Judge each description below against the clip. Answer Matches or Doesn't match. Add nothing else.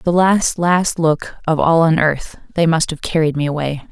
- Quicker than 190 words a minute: Matches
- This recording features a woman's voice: Matches